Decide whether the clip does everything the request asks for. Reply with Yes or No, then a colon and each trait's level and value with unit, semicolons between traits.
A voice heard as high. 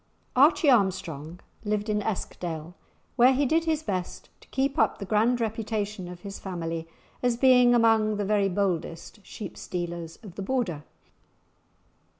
Yes: high, 210 Hz